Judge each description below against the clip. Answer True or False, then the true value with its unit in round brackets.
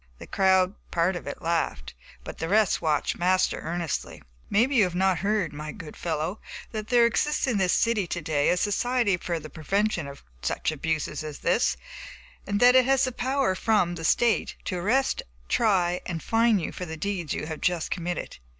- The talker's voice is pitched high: False (180 Hz)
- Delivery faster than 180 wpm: True (190 wpm)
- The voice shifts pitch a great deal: False (4.9 semitones)